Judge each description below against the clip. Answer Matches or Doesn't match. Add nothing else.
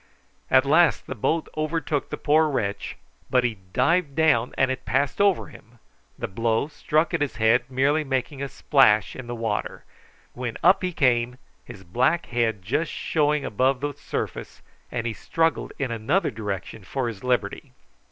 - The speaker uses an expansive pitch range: Doesn't match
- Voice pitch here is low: Matches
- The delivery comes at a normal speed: Matches